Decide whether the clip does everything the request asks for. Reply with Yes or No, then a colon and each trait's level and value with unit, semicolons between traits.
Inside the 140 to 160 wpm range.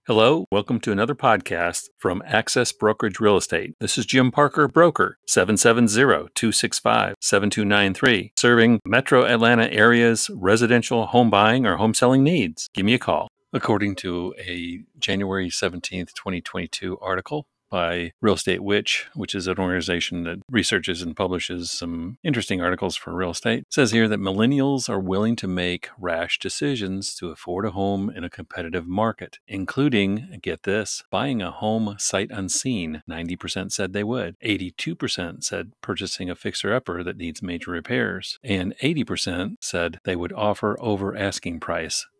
Yes: average, 155 wpm